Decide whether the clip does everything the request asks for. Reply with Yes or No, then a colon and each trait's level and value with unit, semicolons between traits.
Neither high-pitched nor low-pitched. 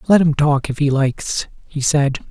Yes: medium, 145 Hz